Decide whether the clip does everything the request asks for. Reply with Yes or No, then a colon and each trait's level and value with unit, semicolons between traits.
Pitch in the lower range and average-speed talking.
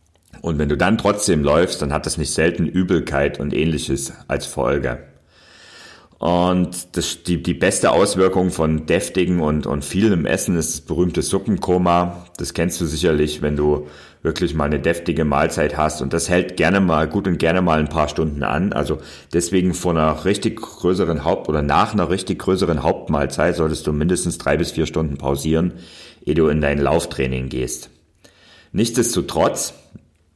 Yes: very low, 80 Hz; average, 165 wpm